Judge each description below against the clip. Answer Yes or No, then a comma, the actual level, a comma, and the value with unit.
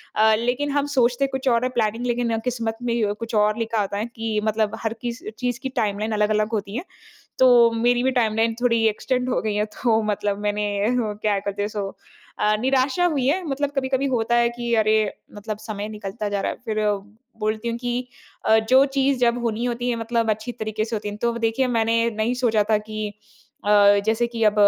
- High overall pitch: Yes, high, 225 Hz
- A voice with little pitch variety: Yes, narrow, 2.3 semitones